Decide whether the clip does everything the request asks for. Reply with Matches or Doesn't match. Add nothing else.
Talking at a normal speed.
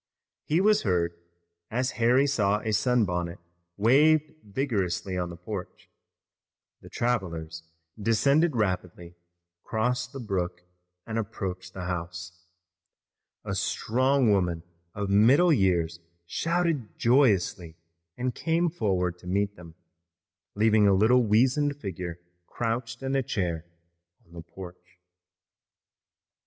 Doesn't match